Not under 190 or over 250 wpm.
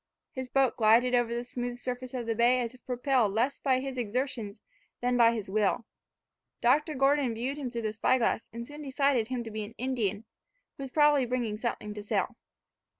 Yes: fast, 205 wpm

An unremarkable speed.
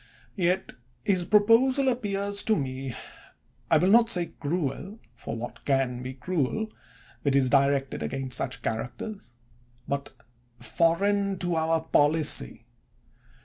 No: slow, 120 wpm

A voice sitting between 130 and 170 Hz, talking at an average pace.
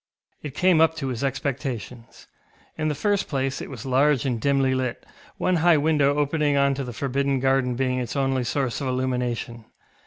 Yes: low, 135 Hz; average, 185 wpm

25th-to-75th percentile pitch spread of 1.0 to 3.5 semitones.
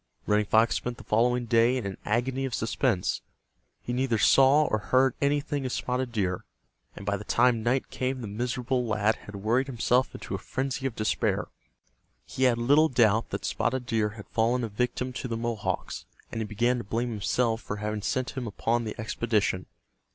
Yes: average, 2.9 semitones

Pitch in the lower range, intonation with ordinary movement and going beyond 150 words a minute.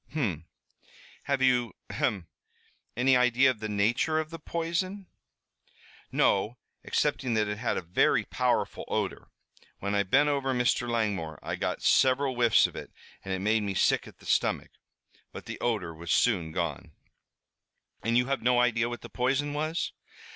Yes: low, 120 Hz; average, 4.6 semitones; average, 165 wpm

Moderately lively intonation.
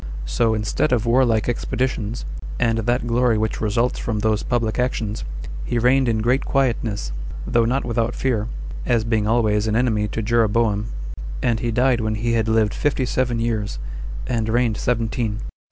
No: narrow, 1.9 semitones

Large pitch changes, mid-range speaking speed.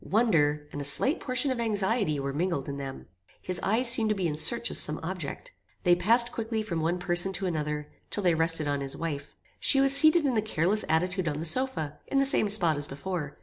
No: wide, 6.8 semitones; fast, 230 wpm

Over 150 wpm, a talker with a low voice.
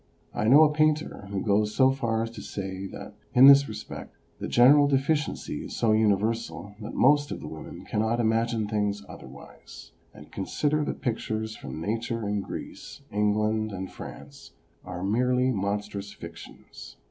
Yes: average, 165 wpm; low, 110 Hz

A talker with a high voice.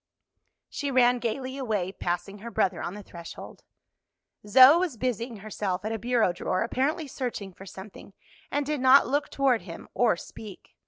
Yes: high, 230 Hz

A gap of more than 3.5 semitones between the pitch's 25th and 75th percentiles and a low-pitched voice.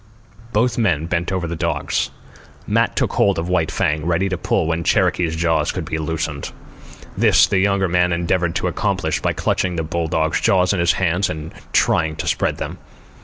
No: narrow, 2.4 semitones; very low, 85 Hz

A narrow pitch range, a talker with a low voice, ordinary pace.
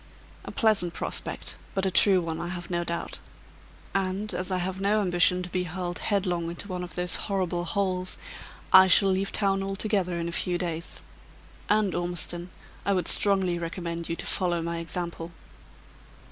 No: narrow, 2.0 semitones; medium, 180 Hz; average, 175 wpm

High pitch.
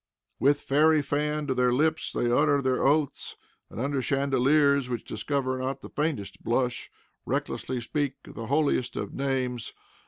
No: low, 135 Hz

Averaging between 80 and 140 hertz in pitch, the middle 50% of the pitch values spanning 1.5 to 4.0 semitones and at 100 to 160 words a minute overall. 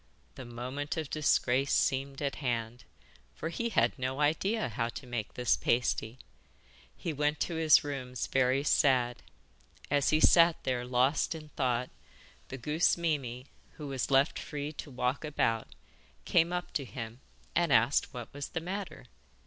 Yes: low, 135 Hz; average, 3.7 semitones; average, 155 wpm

